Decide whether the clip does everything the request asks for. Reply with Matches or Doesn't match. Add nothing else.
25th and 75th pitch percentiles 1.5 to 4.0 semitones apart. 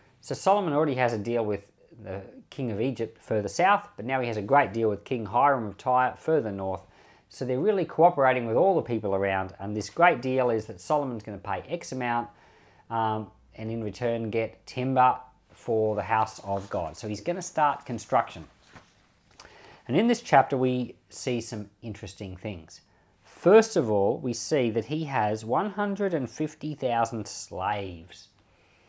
Doesn't match